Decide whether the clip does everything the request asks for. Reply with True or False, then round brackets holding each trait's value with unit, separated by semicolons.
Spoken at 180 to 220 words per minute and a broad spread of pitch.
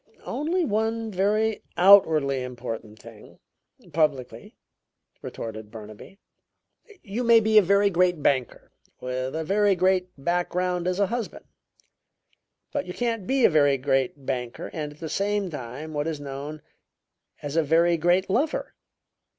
False (140 wpm; 6.6 semitones)